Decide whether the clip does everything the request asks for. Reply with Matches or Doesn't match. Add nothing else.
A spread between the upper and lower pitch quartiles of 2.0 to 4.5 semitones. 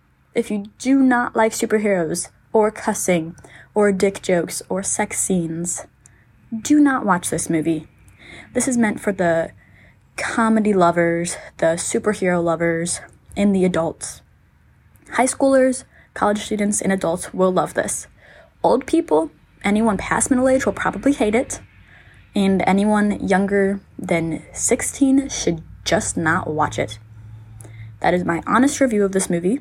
Doesn't match